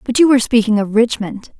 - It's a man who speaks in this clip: No, female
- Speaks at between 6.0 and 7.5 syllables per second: Yes, 6.1 syllables/s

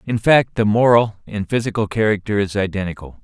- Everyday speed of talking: Yes, average, 165 wpm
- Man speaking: Yes, male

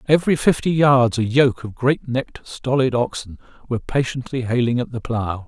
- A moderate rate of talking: Yes, average, 175 wpm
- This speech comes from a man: Yes, male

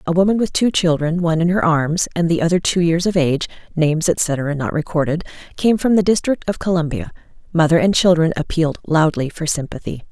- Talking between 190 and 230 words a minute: Yes, average, 195 wpm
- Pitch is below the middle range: No, medium, 170 Hz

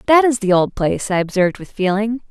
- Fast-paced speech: Yes, fast, 235 wpm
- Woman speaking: Yes, female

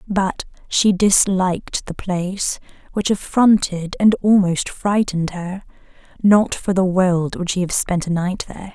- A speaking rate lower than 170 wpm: Yes, average, 150 wpm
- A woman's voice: Yes, female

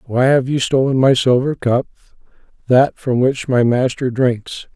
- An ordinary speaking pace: Yes, average, 165 wpm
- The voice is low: Yes, low, 130 Hz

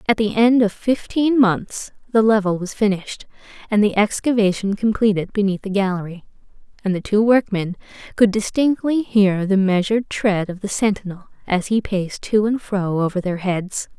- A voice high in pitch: Yes, high, 205 Hz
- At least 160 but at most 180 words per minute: Yes, average, 165 wpm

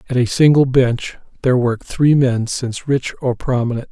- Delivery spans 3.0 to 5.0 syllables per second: No, 5.2 syllables/s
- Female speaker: No, male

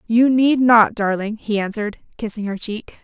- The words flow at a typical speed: Yes, average, 180 wpm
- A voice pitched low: No, high, 220 Hz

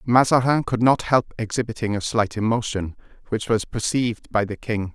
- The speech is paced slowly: No, average, 170 wpm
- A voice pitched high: No, low, 110 Hz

